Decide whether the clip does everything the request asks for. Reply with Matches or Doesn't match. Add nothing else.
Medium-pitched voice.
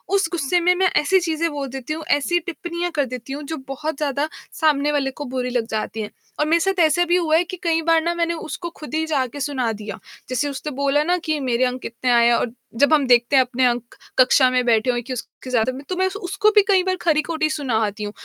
Doesn't match